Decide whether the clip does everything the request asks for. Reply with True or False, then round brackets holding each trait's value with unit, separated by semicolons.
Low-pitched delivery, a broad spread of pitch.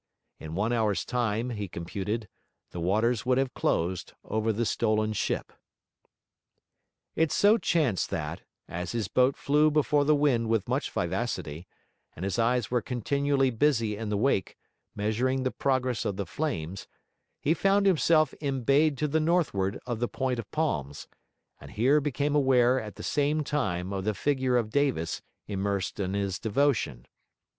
True (120 Hz; 5.8 semitones)